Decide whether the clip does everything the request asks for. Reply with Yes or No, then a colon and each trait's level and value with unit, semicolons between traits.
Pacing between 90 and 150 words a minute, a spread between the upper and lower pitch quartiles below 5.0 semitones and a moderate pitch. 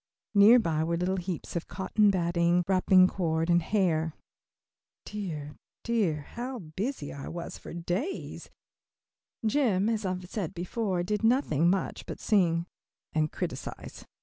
Yes: average, 140 wpm; average, 3.8 semitones; medium, 180 Hz